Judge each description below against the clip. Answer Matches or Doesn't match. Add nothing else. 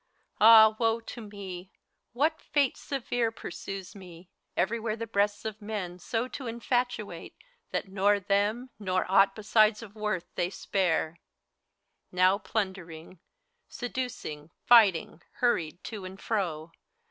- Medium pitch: Doesn't match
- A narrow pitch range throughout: Doesn't match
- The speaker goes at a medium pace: Doesn't match